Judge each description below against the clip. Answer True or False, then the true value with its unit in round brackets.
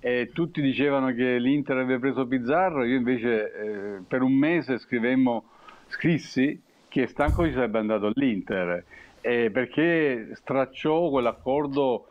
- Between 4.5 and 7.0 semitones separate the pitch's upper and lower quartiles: False (2.8 semitones)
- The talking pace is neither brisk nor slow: True (130 wpm)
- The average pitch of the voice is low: True (130 Hz)